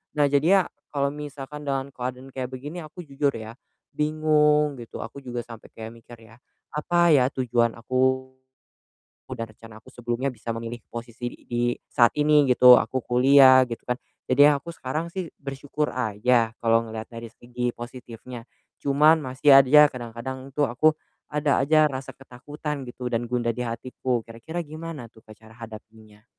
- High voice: No, low, 130 Hz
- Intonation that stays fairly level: No, average, 3.7 semitones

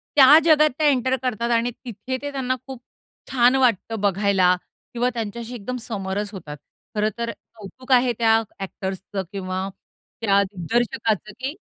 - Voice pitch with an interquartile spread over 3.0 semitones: Yes, average, 4.2 semitones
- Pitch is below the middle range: No, high, 230 Hz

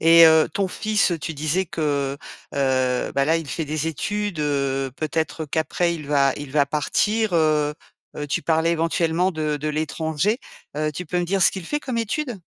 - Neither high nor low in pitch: Yes, medium, 160 Hz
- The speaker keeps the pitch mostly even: No, average, 3.2 semitones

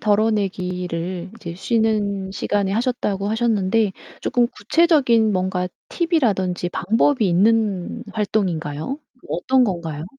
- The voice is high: Yes, high, 205 Hz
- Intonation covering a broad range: No, average, 3.8 semitones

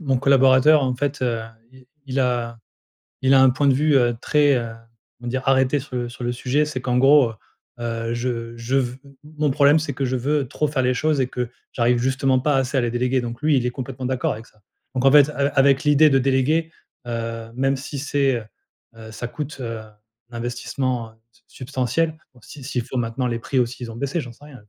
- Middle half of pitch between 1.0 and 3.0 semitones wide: Yes, narrow, 2.5 semitones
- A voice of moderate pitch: No, low, 130 Hz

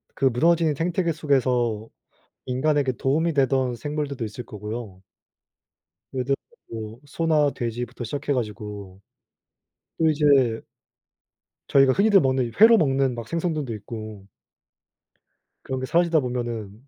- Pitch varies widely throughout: No, average, 4.5 semitones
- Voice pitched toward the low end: Yes, low, 130 Hz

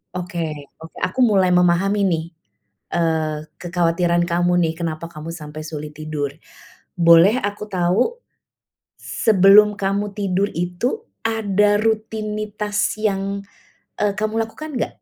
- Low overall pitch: No, medium, 185 Hz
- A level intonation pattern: No, average, 3.7 semitones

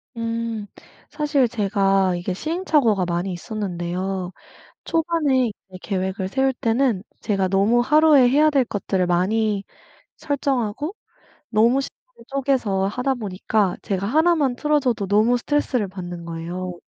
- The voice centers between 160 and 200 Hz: No, high, 220 Hz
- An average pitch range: No, wide, 6.1 semitones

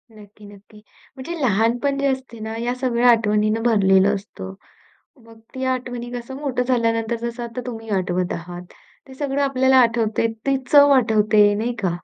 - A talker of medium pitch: No, high, 230 Hz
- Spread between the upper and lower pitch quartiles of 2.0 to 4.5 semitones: Yes, average, 3.4 semitones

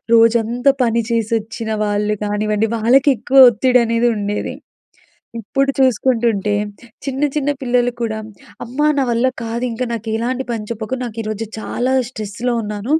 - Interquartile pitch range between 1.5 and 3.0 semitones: Yes, narrow, 2.6 semitones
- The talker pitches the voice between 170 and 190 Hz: No, high, 230 Hz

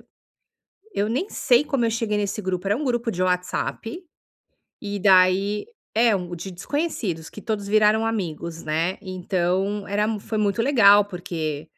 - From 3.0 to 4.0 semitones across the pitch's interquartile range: Yes, average, 3.5 semitones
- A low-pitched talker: No, high, 205 Hz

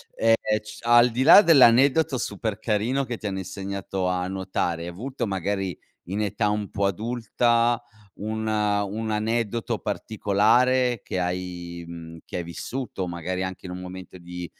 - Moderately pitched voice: No, low, 105 Hz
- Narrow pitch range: No, average, 4.2 semitones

